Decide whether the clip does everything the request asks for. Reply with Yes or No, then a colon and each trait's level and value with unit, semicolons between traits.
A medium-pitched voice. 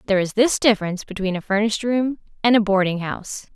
No: high, 210 Hz